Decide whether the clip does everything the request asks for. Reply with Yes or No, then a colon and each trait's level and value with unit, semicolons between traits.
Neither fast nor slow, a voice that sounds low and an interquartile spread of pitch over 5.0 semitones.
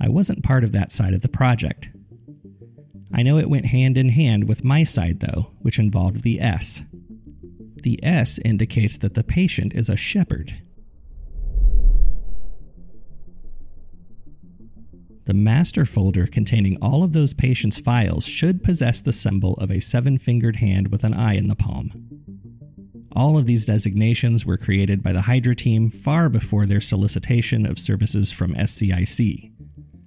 No: average, 150 wpm; low, 110 Hz; average, 4.2 semitones